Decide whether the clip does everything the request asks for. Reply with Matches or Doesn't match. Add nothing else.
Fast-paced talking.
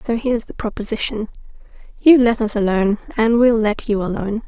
Doesn't match